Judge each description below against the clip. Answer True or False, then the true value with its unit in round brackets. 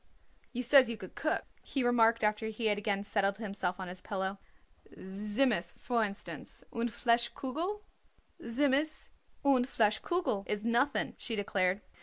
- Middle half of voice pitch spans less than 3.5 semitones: False (3.9 semitones)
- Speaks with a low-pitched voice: False (225 Hz)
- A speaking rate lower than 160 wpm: True (150 wpm)